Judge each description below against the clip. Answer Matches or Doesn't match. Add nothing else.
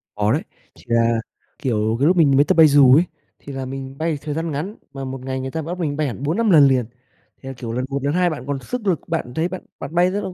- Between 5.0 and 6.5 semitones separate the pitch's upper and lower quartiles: Doesn't match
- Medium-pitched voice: Matches